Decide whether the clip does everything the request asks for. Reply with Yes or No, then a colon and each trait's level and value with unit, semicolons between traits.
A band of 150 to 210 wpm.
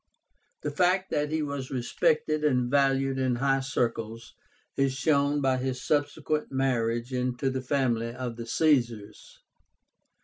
No: slow, 135 wpm